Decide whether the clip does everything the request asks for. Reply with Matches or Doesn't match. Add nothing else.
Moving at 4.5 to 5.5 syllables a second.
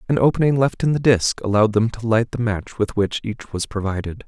Doesn't match